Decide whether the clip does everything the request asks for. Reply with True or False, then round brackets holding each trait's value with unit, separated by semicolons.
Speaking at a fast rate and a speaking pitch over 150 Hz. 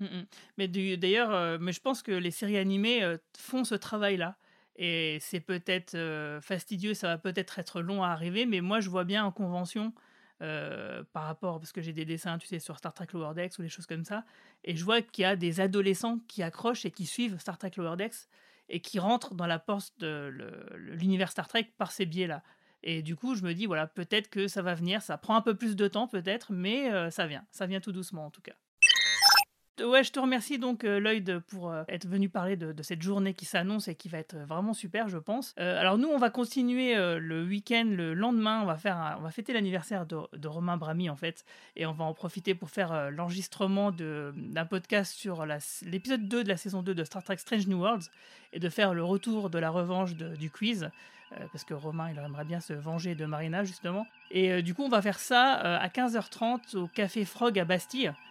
True (240 wpm; 190 Hz)